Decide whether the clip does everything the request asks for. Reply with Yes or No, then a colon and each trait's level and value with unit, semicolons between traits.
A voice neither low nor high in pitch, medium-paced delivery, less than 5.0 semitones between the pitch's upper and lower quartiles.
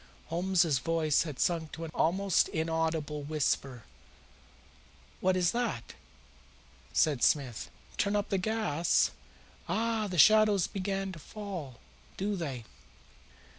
No: medium, 170 Hz; slow, 115 wpm; average, 4.6 semitones